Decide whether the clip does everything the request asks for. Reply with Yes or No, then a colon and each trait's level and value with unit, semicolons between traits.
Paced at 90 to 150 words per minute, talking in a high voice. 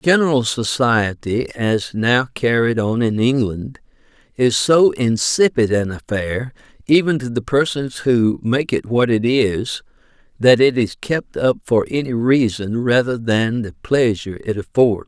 No: average, 145 wpm; low, 120 Hz